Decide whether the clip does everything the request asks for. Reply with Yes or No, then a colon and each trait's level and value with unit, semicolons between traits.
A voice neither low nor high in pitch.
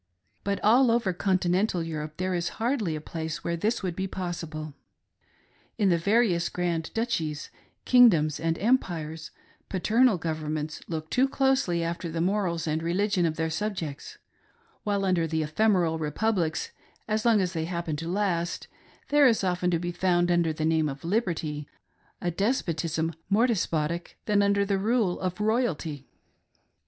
Yes: medium, 175 Hz